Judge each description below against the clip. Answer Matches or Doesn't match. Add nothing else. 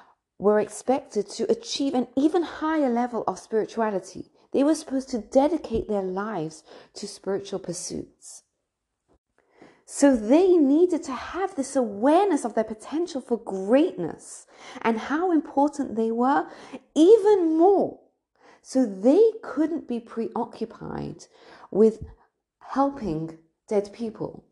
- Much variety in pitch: Matches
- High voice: Matches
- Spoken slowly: Matches